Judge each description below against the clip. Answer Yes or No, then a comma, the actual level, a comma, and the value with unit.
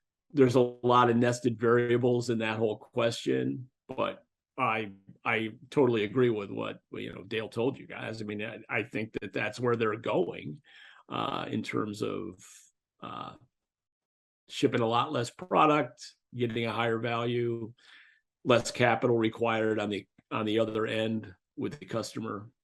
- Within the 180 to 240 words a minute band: No, average, 155 wpm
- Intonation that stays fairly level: Yes, narrow, 1.8 semitones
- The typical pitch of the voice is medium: No, low, 115 Hz